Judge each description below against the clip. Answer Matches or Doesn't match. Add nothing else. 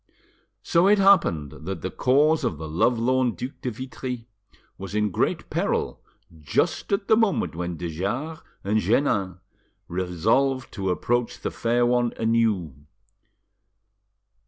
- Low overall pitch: Matches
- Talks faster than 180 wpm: Doesn't match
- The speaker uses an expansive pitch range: Matches